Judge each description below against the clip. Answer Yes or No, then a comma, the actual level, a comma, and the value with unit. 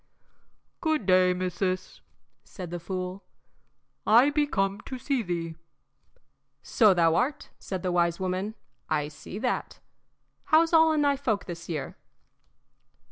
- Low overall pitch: No, high, 190 Hz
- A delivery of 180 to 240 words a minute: No, slow, 135 wpm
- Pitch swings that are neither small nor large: No, wide, 6.5 semitones